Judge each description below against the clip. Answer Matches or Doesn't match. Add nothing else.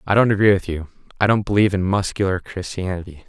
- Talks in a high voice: Doesn't match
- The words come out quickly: Doesn't match